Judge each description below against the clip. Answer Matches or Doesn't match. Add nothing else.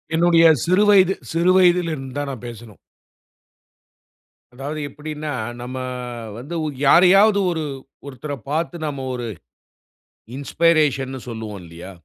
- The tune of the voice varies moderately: Matches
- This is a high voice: Doesn't match